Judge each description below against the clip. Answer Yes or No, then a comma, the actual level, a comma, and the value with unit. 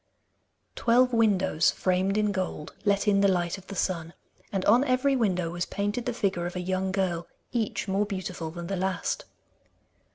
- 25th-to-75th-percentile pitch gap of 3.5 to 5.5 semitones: No, average, 2.7 semitones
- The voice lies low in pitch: No, high, 190 Hz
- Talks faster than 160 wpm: Yes, average, 175 wpm